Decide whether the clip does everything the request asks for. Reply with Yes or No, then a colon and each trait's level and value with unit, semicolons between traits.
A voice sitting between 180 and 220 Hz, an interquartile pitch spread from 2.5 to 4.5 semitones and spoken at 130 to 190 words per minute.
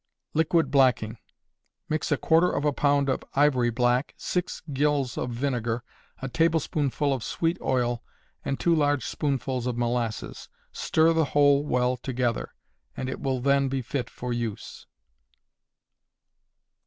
No: low, 135 Hz; average, 3.1 semitones; average, 140 wpm